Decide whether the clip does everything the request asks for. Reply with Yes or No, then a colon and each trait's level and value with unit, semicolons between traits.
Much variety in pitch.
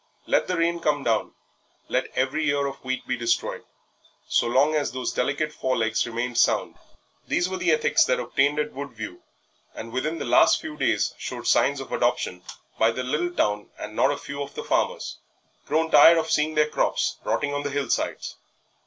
No: average, 3.7 semitones